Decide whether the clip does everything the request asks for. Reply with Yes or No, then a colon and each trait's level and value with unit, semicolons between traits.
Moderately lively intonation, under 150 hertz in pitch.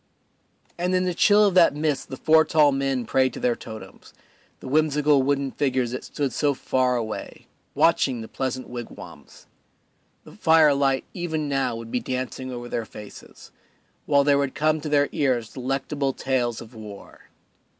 Yes: average, 3.1 semitones; low, 135 Hz